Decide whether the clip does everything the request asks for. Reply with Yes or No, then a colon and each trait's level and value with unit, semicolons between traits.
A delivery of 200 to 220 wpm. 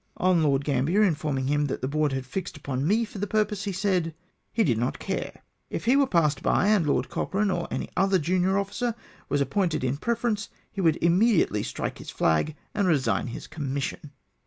Yes: fast, 205 wpm